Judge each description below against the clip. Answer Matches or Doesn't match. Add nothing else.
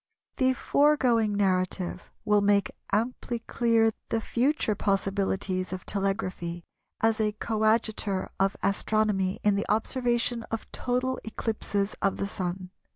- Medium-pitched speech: Doesn't match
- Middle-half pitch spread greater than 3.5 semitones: Doesn't match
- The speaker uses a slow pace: Matches